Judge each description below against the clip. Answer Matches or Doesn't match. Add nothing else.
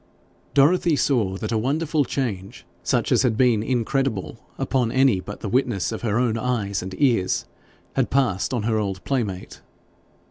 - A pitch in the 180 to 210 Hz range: Doesn't match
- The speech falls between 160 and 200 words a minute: Matches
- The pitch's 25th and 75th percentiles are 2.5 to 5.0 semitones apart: Matches